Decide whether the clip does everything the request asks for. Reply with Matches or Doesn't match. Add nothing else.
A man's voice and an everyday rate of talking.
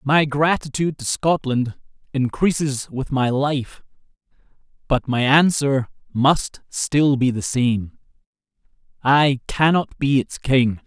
Doesn't match